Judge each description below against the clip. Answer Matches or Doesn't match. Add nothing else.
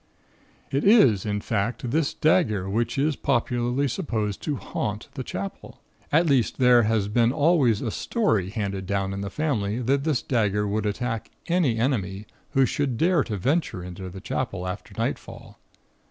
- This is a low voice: Matches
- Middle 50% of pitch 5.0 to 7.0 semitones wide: Matches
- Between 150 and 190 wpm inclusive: Matches